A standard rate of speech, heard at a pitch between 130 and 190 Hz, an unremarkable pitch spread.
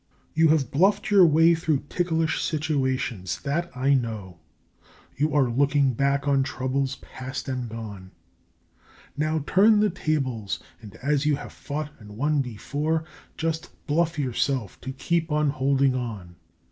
Yes: average, 145 wpm; medium, 140 Hz; average, 3.6 semitones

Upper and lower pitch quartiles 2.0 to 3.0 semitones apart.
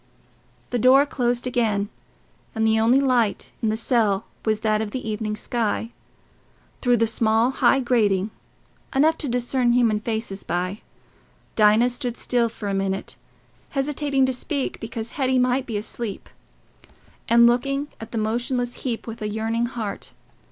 Yes: narrow, 2.6 semitones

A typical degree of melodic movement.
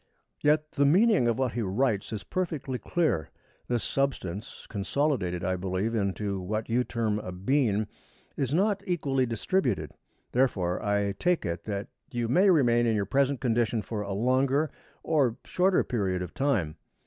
No: wide, 5.7 semitones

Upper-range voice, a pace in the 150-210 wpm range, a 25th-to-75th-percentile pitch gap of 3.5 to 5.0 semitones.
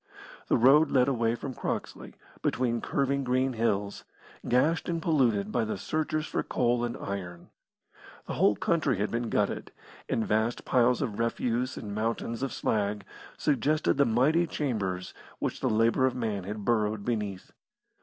No: low, 120 Hz; average, 155 wpm; average, 3.9 semitones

